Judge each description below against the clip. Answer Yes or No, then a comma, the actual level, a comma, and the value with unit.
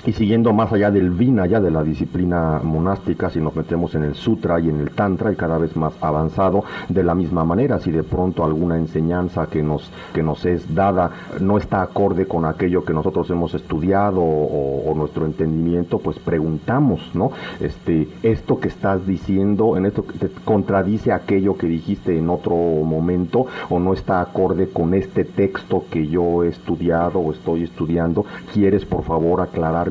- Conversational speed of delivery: Yes, average, 180 wpm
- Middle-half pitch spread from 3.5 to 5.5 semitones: No, average, 3.1 semitones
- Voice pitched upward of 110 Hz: No, very low, 85 Hz